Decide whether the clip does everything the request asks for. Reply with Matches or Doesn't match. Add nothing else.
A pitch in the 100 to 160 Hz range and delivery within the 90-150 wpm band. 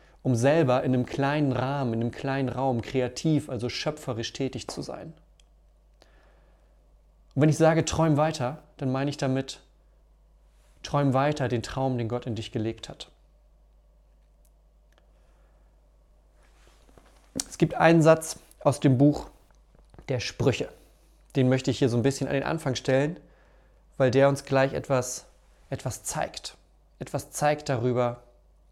Matches